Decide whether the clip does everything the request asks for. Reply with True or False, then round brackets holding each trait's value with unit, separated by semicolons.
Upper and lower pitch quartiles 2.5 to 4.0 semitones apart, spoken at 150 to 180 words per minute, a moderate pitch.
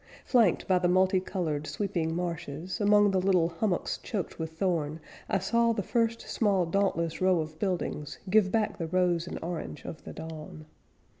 True (3.5 semitones; 170 wpm; 180 Hz)